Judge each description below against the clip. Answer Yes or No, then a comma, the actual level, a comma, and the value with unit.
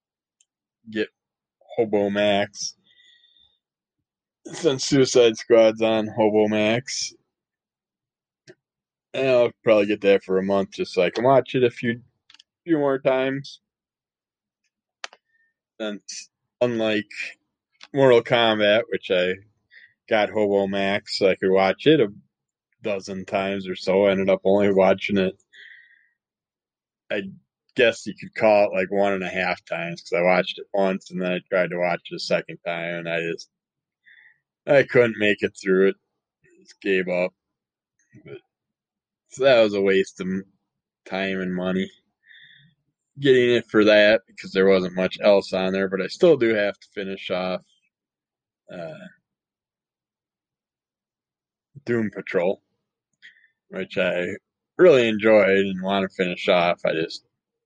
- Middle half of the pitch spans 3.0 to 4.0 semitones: Yes, average, 3.3 semitones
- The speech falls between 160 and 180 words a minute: No, average, 140 wpm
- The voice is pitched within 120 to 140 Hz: No, low, 100 Hz